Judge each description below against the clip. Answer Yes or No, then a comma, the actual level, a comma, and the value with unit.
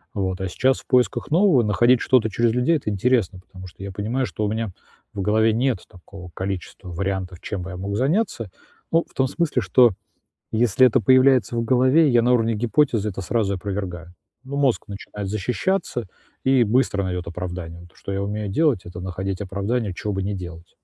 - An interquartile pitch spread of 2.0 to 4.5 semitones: No, average, 4.9 semitones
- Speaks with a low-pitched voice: Yes, low, 105 Hz